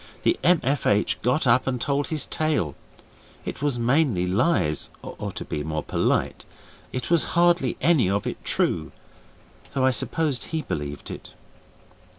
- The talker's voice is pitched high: No, low, 130 Hz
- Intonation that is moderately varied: No, wide, 7.3 semitones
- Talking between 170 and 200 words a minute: No, average, 150 wpm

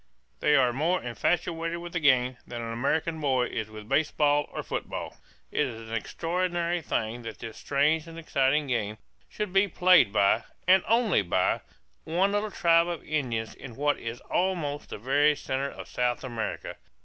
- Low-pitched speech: No, medium, 145 Hz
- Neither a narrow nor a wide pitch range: No, wide, 5.9 semitones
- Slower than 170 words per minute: No, average, 175 wpm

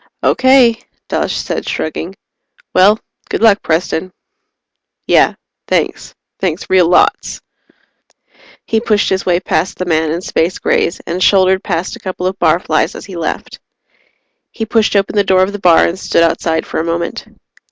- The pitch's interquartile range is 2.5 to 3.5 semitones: Yes, average, 3.0 semitones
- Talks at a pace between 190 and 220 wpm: No, average, 160 wpm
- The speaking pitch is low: No, medium, 185 Hz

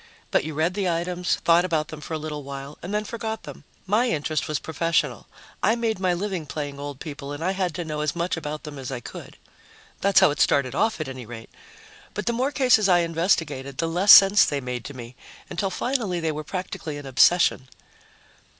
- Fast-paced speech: Yes, fast, 215 wpm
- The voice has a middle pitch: Yes, medium, 165 Hz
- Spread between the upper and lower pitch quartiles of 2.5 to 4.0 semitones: No, average, 4.7 semitones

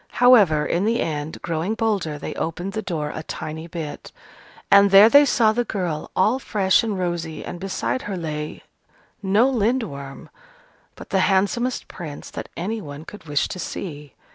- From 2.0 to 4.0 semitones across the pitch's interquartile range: No, wide, 5.5 semitones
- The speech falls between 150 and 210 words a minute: Yes, average, 165 wpm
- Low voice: No, medium, 185 Hz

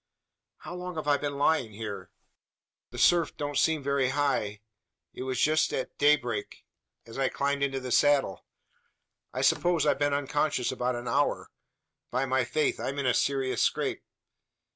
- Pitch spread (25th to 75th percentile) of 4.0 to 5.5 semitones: No, narrow, 2.4 semitones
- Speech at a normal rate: Yes, average, 160 wpm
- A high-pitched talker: No, medium, 140 Hz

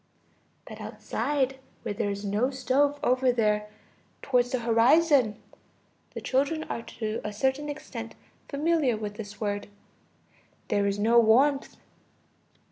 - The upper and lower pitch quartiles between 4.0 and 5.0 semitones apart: Yes, average, 4.6 semitones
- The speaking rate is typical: No, slow, 125 wpm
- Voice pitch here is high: Yes, high, 245 Hz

